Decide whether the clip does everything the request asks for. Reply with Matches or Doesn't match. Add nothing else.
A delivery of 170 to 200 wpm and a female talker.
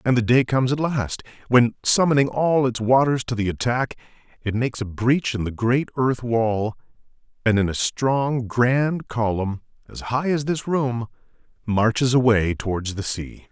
Doesn't match